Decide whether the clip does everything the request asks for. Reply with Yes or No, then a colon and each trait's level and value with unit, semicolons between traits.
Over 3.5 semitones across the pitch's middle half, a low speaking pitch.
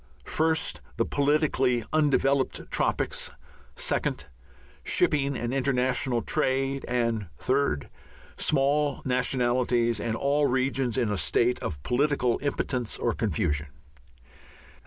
No: average, 2.7 semitones; low, 130 Hz